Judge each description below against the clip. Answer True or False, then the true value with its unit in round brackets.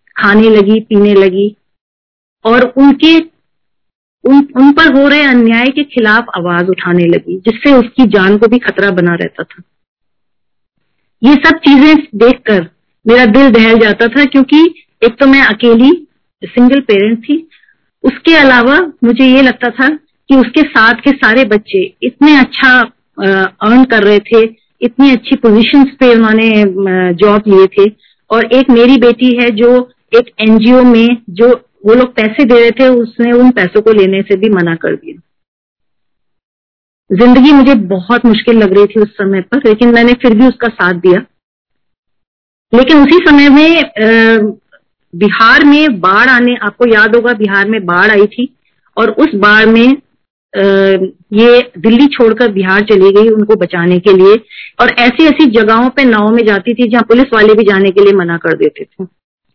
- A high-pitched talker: True (235 Hz)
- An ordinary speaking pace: True (165 wpm)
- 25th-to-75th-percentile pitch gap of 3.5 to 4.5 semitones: True (4.1 semitones)